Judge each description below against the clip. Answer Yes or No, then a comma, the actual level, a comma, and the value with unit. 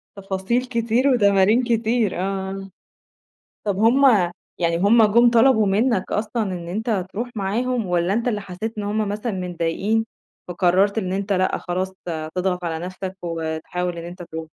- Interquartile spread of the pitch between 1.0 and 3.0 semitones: No, average, 3.9 semitones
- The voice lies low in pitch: No, high, 195 Hz